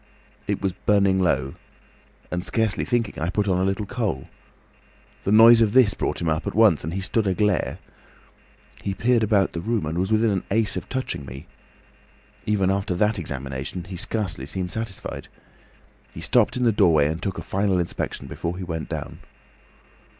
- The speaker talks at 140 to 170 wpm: No, average, 180 wpm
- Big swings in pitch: No, average, 3.8 semitones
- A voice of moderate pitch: No, very low, 95 Hz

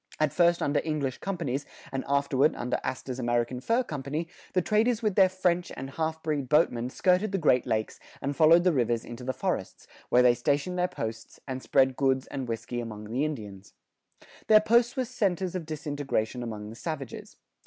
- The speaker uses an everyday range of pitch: No, wide, 5.8 semitones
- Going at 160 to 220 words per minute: Yes, average, 185 wpm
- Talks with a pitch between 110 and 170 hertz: Yes, medium, 140 Hz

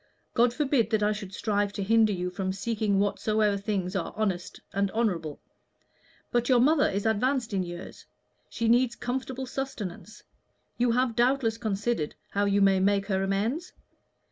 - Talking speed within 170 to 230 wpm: No, average, 160 wpm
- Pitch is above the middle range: Yes, high, 215 Hz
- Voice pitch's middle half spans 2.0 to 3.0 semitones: No, average, 3.5 semitones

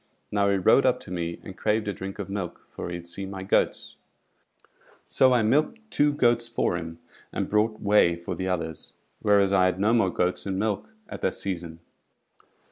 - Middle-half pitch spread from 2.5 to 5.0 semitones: Yes, average, 3.4 semitones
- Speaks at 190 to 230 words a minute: Yes, average, 200 wpm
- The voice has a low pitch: Yes, low, 100 Hz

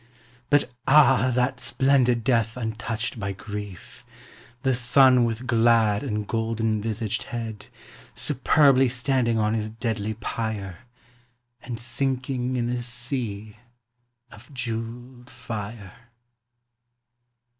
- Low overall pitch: Yes, low, 115 Hz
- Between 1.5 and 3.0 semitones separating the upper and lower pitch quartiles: Yes, narrow, 2.4 semitones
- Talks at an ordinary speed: No, slow, 100 wpm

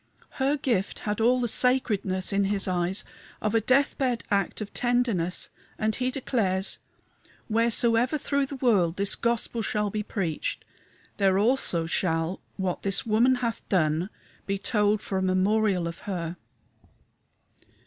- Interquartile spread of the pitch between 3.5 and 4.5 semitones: Yes, average, 4.1 semitones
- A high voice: Yes, high, 210 Hz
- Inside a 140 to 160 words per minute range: Yes, average, 145 wpm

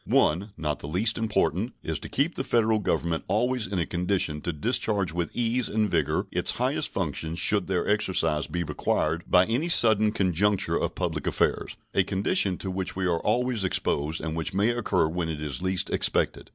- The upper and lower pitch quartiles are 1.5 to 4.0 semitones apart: No, average, 4.6 semitones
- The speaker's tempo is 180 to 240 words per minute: Yes, average, 190 wpm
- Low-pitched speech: Yes, very low, 95 Hz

